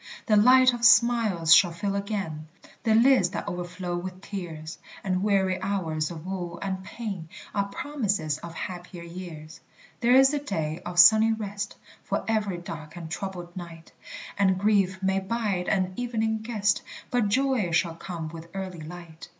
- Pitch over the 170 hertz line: Yes, high, 190 Hz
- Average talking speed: Yes, average, 160 wpm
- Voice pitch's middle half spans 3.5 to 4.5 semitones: Yes, average, 3.8 semitones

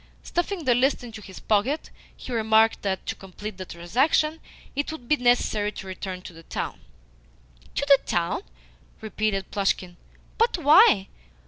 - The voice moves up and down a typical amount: No, wide, 6.4 semitones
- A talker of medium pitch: No, high, 220 Hz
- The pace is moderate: Yes, average, 150 wpm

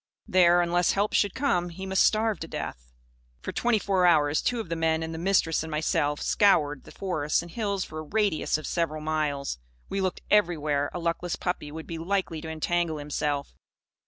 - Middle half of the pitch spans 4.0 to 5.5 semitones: No, average, 3.6 semitones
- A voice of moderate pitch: Yes, medium, 165 Hz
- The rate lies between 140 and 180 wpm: No, average, 195 wpm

